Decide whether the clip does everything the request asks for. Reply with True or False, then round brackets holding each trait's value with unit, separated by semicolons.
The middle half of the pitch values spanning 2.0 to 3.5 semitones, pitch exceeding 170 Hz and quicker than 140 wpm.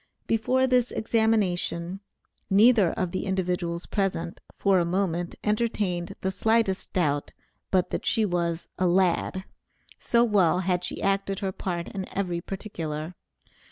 False (3.1 semitones; 190 Hz; 135 wpm)